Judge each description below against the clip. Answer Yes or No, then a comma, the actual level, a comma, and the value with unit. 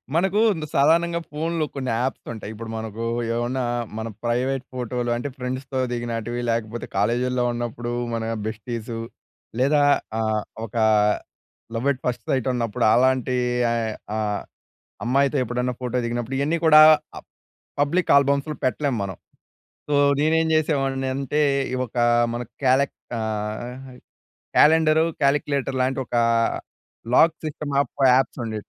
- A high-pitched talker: No, low, 125 Hz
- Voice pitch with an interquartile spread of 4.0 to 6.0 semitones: No, average, 3.2 semitones